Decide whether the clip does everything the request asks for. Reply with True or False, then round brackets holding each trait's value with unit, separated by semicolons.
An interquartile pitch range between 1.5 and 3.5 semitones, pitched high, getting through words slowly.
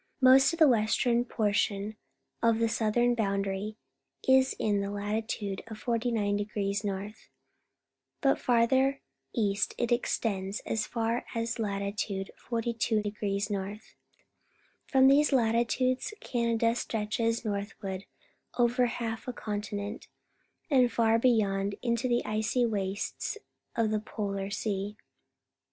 True (2.8 semitones; 220 Hz; 110 wpm)